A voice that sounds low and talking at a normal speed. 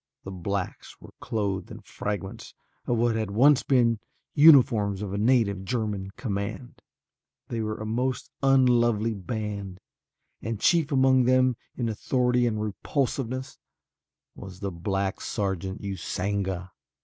No: low, 110 Hz; slow, 125 wpm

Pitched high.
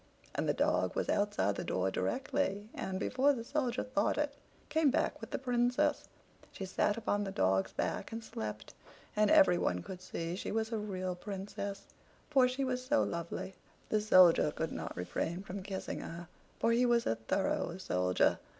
Yes: high, 205 Hz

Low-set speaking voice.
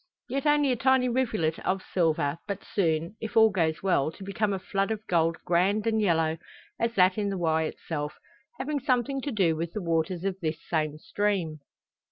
No: high, 190 Hz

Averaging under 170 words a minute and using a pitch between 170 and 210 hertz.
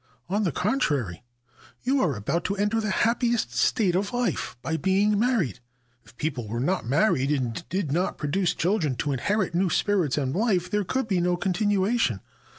No: average, 180 wpm; medium, 185 Hz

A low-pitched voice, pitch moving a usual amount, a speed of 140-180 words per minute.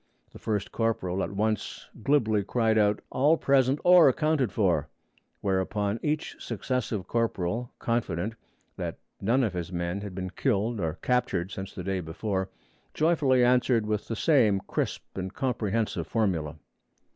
Yes: low, 110 Hz; average, 4.5 semitones; average, 145 wpm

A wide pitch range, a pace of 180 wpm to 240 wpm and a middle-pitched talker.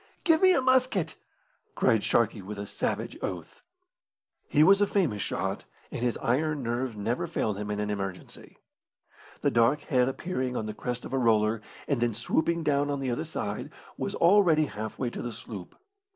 No: wide, 6.5 semitones; average, 185 wpm; low, 125 Hz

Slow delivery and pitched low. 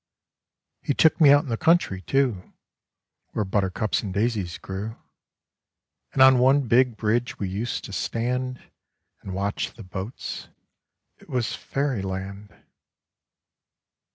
Yes: slow, 125 wpm; low, 115 Hz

